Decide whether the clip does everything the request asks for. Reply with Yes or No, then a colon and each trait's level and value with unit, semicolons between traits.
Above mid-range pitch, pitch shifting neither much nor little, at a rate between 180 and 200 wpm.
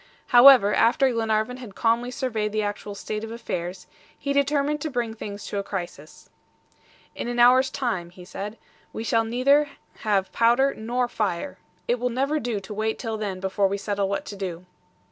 Yes: high, 225 Hz; average, 3.6 semitones; average, 185 wpm